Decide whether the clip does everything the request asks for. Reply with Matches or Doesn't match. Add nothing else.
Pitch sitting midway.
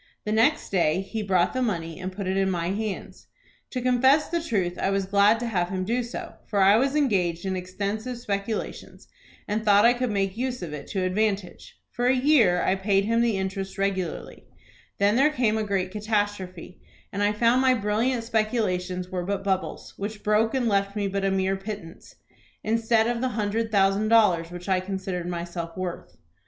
Doesn't match